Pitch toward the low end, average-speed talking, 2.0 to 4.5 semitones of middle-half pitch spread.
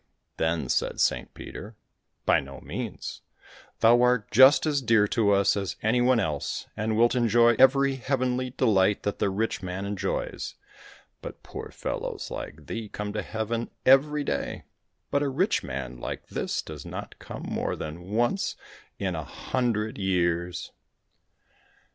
No: low, 110 Hz; average, 150 wpm; average, 5.2 semitones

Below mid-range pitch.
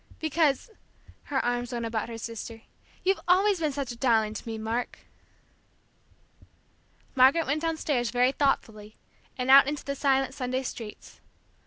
No: very high, 260 Hz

